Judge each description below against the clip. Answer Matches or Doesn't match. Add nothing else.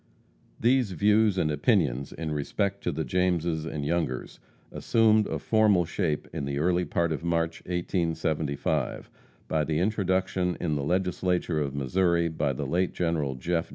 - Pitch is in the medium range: Doesn't match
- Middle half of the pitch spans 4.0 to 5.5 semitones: Doesn't match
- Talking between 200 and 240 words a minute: Doesn't match